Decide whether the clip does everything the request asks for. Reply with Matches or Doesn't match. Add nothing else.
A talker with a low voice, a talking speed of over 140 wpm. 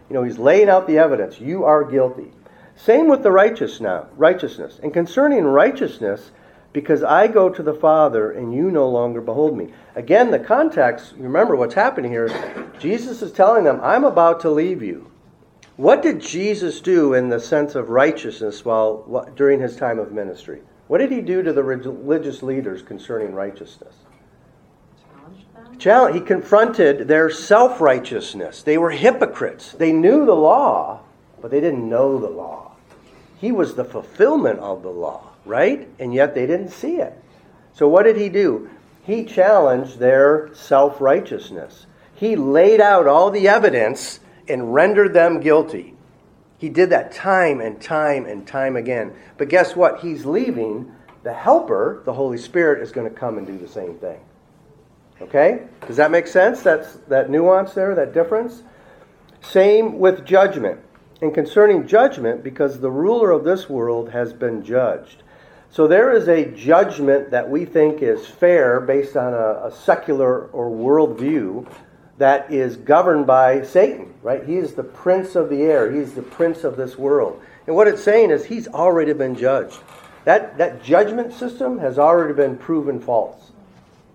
Doesn't match